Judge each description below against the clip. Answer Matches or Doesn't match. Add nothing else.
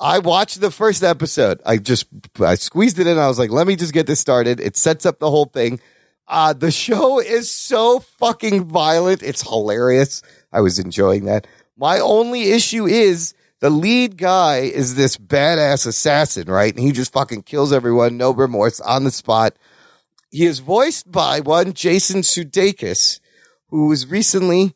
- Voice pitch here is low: Doesn't match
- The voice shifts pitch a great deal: Matches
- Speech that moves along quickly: Doesn't match